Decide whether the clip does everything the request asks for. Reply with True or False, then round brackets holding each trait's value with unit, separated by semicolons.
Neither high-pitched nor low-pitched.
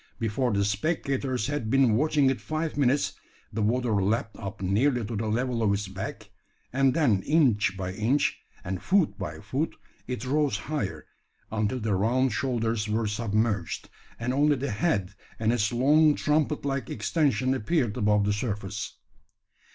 False (120 Hz)